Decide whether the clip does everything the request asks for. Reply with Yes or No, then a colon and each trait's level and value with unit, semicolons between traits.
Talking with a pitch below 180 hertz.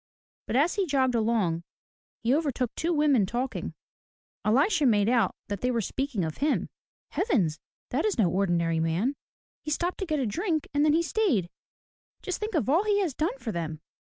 No: very high, 260 Hz